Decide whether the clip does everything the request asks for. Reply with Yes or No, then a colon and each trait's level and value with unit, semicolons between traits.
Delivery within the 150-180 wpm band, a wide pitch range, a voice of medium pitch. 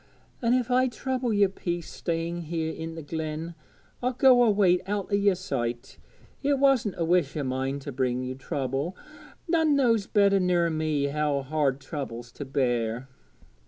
Yes: average, 165 wpm; wide, 6.8 semitones; medium, 165 Hz